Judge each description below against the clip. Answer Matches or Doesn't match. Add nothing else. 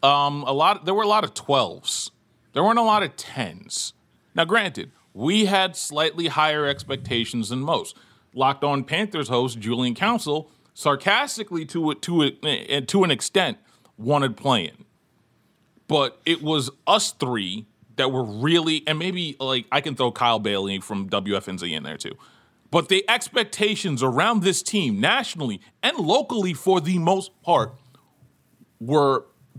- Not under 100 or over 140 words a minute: Doesn't match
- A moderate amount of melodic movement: Doesn't match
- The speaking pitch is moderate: Matches